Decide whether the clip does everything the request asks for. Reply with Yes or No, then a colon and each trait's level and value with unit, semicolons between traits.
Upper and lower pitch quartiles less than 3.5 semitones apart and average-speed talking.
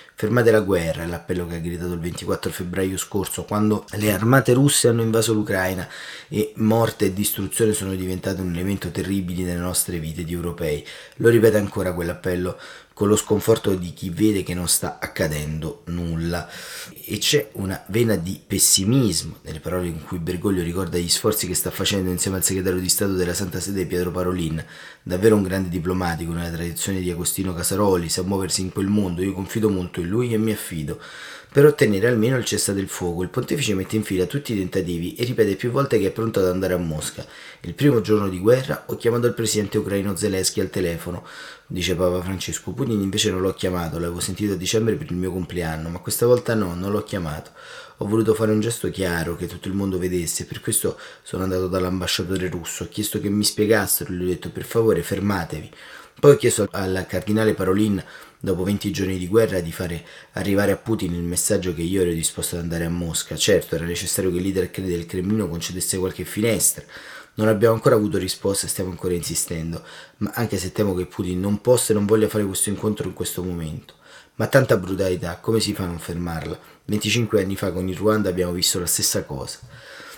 No: average, 2.9 semitones; fast, 200 wpm